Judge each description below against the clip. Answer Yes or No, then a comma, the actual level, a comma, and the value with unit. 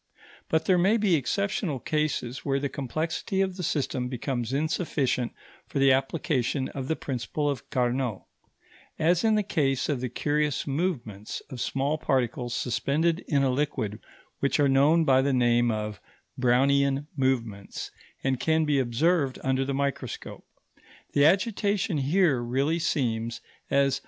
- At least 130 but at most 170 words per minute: Yes, average, 150 wpm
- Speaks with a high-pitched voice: No, medium, 140 Hz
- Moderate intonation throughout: Yes, average, 3.8 semitones